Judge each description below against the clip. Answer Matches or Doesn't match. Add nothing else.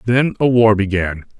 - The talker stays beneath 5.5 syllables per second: Matches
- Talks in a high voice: Doesn't match